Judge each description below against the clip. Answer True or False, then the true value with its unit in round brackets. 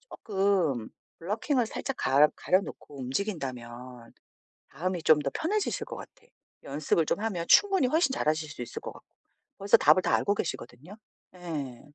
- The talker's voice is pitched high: False (170 Hz)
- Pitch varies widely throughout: True (7.3 semitones)